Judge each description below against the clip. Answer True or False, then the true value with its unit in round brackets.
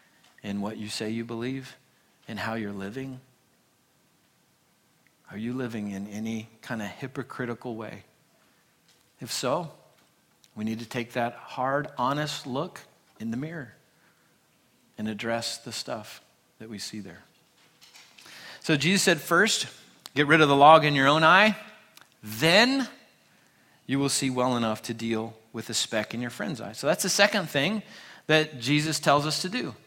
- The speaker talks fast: False (160 wpm)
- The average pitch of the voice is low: True (130 Hz)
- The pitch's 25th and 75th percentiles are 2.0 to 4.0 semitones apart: False (5.4 semitones)